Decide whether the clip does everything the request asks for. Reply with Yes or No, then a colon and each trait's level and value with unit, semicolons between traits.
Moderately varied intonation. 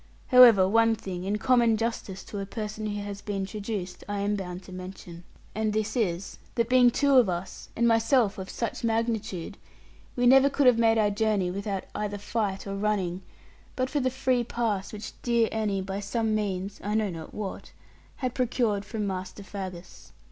Yes: average, 3.0 semitones